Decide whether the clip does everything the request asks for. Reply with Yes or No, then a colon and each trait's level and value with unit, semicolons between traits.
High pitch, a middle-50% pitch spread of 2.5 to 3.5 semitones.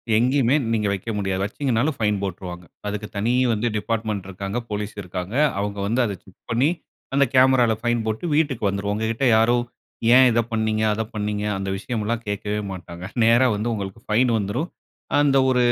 No: low, 110 Hz; average, 2.9 semitones